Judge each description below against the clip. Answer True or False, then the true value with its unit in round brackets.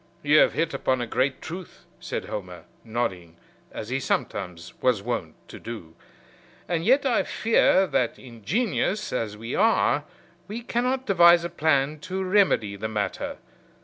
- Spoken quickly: False (150 wpm)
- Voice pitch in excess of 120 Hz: True (135 Hz)